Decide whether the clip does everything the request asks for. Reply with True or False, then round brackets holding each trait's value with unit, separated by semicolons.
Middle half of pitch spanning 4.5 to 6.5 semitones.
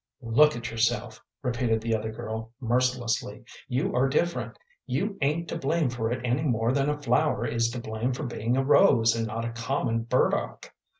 False (3.0 semitones)